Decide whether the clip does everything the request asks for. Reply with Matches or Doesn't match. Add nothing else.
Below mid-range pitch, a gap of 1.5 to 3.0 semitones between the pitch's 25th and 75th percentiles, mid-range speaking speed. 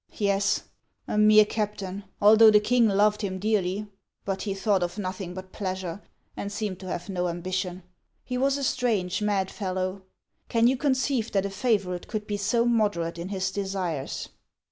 Doesn't match